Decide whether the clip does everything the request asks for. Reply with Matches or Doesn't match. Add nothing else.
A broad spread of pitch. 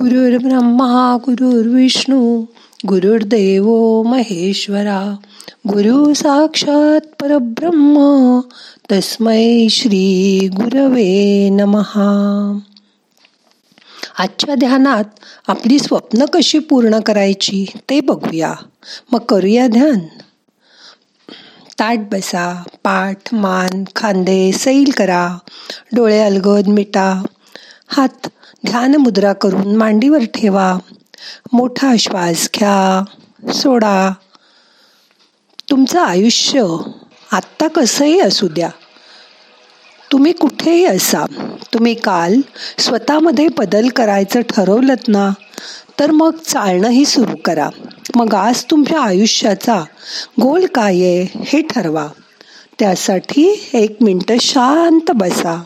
Doesn't match